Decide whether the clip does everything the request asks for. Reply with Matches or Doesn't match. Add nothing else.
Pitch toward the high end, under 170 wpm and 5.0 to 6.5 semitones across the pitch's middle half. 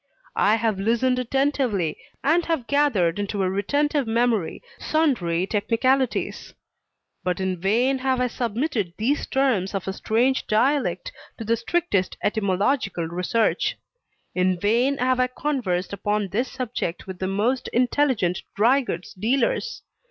Matches